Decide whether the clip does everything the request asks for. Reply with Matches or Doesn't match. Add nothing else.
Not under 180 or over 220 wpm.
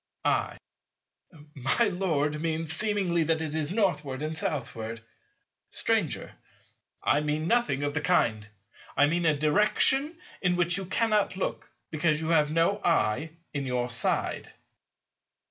Doesn't match